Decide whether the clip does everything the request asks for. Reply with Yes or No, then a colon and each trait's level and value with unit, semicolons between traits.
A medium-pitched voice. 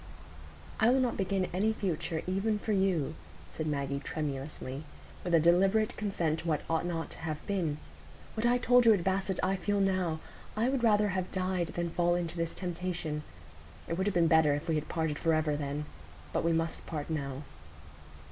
Yes: medium, 175 Hz